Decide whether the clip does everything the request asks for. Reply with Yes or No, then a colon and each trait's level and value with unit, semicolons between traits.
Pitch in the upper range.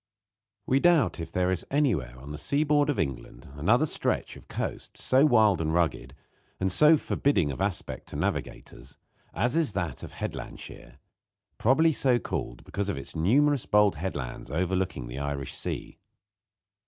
No: very low, 95 Hz